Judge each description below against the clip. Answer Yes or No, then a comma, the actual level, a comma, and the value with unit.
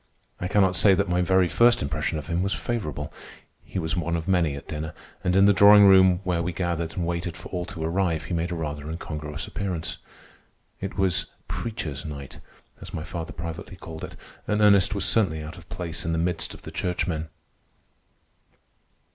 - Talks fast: No, average, 195 wpm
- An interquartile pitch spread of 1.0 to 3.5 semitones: Yes, average, 2.9 semitones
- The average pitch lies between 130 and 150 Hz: No, very low, 85 Hz